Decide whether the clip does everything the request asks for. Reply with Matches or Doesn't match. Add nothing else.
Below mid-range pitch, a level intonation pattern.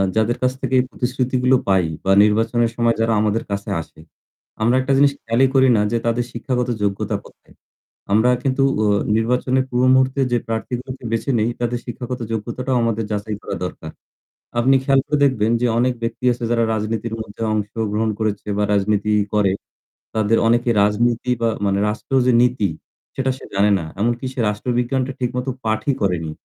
Doesn't match